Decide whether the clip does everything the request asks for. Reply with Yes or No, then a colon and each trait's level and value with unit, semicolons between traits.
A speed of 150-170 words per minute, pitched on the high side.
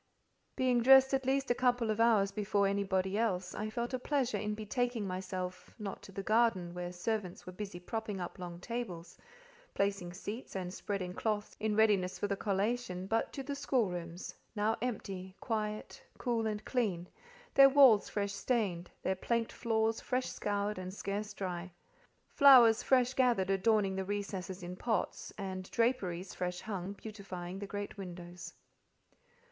Yes: average, 155 wpm; high, 205 Hz